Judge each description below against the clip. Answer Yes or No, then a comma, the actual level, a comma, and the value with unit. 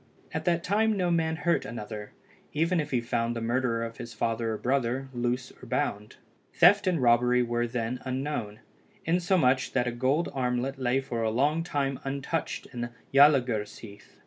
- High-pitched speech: No, low, 125 Hz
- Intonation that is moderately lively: Yes, average, 4.1 semitones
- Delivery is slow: No, average, 170 wpm